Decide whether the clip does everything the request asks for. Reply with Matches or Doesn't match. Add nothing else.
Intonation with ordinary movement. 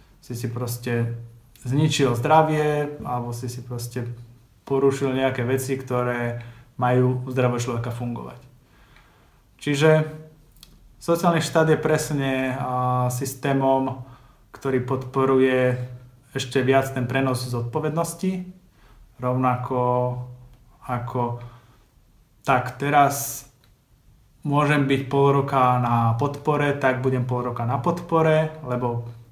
Doesn't match